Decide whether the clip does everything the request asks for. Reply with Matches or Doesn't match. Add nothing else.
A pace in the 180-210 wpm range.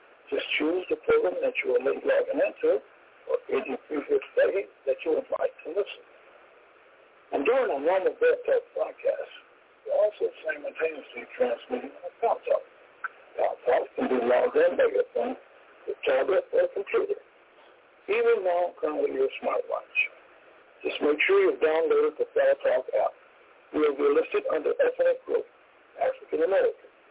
Doesn't match